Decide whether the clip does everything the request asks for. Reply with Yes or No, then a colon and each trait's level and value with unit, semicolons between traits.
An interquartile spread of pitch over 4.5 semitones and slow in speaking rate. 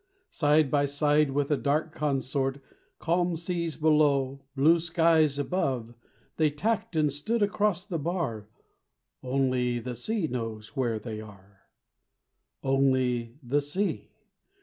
No: average, 4.2 semitones; slow, 125 wpm